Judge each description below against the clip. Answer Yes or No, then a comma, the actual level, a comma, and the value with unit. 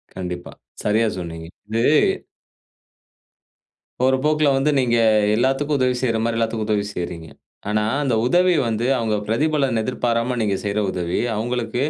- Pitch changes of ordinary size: Yes, average, 3.5 semitones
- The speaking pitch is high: No, low, 115 Hz